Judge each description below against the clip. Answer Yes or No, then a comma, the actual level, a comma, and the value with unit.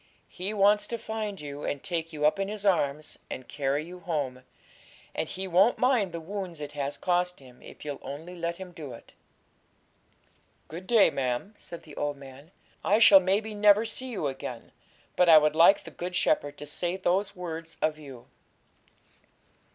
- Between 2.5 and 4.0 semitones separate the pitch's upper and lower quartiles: No, average, 5.1 semitones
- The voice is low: No, medium, 170 Hz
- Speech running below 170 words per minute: No, average, 180 wpm